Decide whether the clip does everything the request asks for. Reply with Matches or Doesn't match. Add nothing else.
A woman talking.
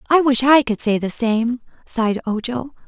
Matches